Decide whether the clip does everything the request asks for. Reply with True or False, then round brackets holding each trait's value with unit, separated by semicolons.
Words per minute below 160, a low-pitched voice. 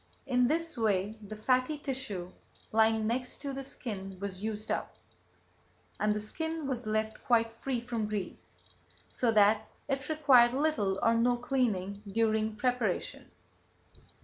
False (140 wpm; 230 Hz)